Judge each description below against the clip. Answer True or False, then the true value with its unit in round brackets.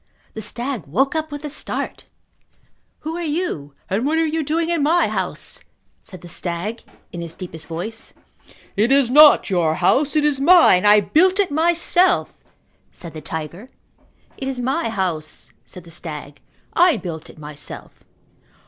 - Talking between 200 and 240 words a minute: False (165 wpm)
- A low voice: False (240 Hz)